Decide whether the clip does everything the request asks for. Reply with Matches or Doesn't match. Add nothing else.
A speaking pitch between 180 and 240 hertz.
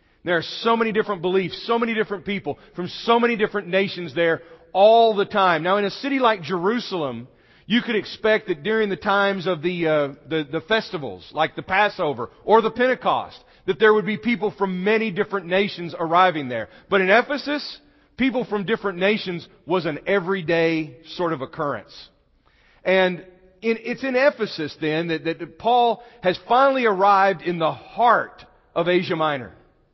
Matches